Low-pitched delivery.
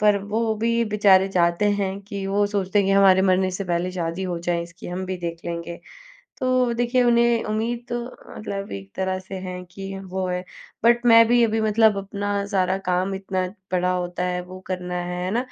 No: high, 190 Hz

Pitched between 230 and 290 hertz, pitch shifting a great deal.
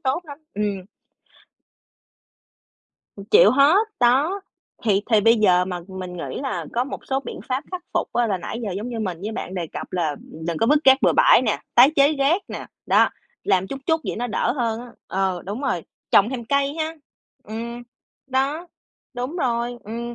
Yes: high, 235 Hz; wide, 5.7 semitones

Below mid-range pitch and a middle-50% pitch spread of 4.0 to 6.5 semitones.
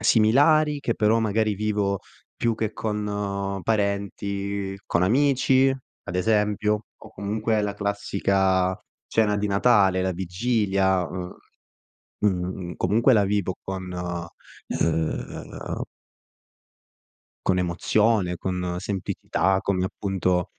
No: low, 100 Hz; narrow, 2.5 semitones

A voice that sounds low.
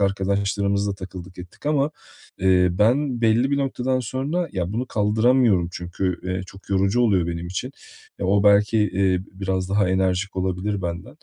Yes: low, 100 Hz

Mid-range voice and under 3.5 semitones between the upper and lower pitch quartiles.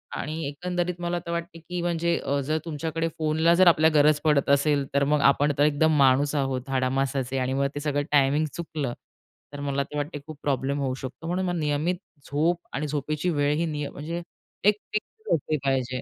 Yes: medium, 150 Hz; average, 2.9 semitones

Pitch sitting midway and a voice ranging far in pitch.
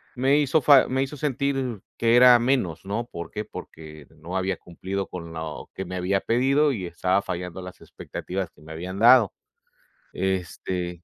No: very low, 95 Hz; wide, 6.1 semitones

